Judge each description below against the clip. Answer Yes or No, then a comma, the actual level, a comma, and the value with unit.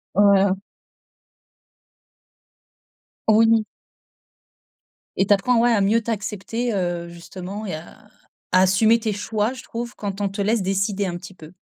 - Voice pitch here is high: Yes, high, 205 Hz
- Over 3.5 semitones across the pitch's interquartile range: No, average, 2.7 semitones